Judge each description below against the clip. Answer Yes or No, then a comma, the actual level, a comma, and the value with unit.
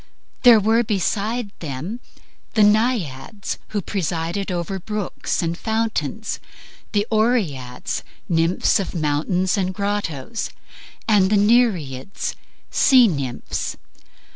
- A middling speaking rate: No, slow, 100 wpm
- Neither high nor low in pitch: No, high, 200 Hz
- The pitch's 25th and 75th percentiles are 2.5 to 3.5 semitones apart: No, average, 4.9 semitones